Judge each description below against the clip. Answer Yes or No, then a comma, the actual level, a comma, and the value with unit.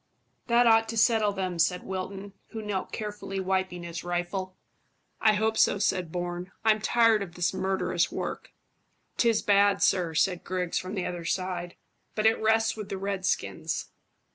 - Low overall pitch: No, high, 190 Hz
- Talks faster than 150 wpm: Yes, average, 165 wpm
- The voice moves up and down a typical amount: Yes, average, 3.1 semitones